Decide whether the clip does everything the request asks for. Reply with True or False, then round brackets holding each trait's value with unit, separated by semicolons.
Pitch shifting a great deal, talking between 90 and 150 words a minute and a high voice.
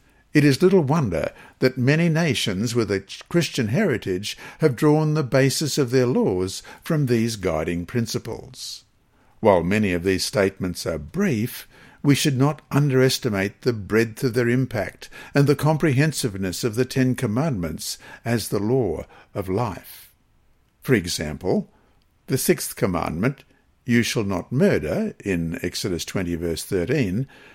False (6.4 semitones; 140 wpm; 125 Hz)